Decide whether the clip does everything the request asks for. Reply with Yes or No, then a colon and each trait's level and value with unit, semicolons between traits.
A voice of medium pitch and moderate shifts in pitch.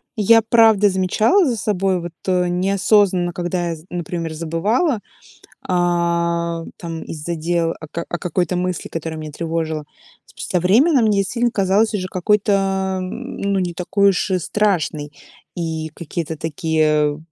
Yes: medium, 180 Hz; average, 3.1 semitones